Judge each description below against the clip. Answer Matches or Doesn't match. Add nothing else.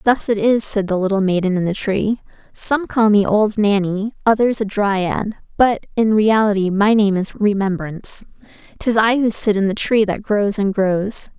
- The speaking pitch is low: Doesn't match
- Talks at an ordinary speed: Matches